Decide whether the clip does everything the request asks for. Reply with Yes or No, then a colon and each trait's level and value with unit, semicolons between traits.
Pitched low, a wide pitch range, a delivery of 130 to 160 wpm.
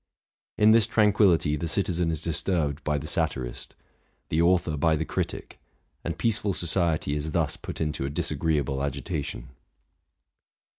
No: very low, 80 Hz; average, 3.0 semitones; average, 145 wpm